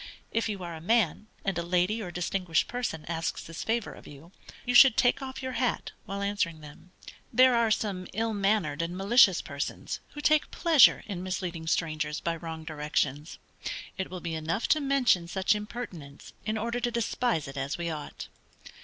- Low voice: No, medium, 185 Hz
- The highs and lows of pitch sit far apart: Yes, wide, 5.9 semitones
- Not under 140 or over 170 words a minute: No, average, 185 wpm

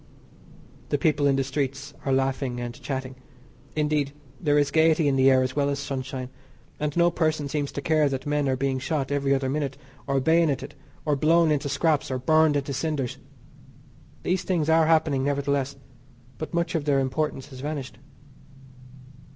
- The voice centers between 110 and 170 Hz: Yes, medium, 140 Hz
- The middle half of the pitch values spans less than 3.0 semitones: Yes, narrow, 2.4 semitones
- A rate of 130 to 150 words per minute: No, average, 175 wpm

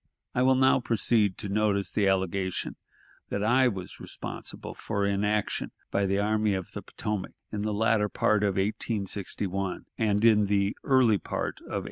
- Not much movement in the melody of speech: Yes, narrow, 1.8 semitones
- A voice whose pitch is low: Yes, low, 105 Hz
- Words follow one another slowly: No, average, 165 wpm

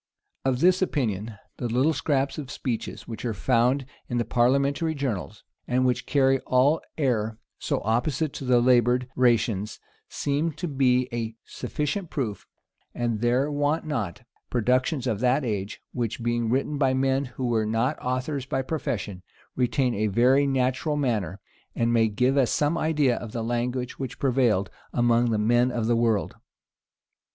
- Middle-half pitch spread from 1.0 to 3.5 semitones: Yes, average, 2.9 semitones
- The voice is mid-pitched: No, low, 125 Hz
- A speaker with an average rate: Yes, average, 160 wpm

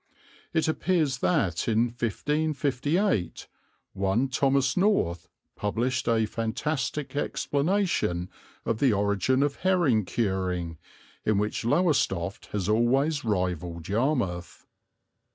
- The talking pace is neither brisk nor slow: No, slow, 100 wpm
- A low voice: Yes, low, 120 Hz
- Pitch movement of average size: No, wide, 6.9 semitones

